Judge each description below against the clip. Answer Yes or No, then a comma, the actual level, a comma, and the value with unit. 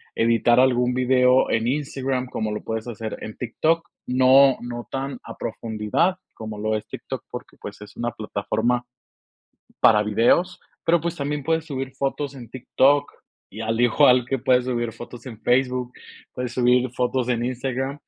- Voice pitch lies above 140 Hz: No, low, 125 Hz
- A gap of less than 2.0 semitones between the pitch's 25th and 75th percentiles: No, narrow, 2.4 semitones